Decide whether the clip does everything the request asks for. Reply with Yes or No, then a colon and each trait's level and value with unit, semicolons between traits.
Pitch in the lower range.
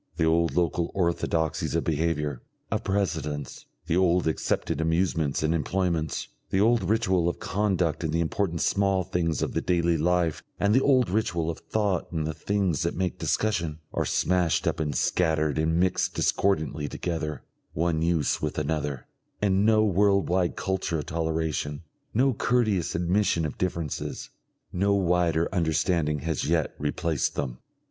Yes: very low, 85 Hz